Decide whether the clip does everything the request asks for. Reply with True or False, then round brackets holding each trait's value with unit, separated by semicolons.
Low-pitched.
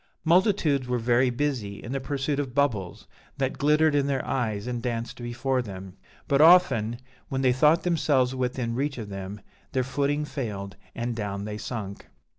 True (125 Hz)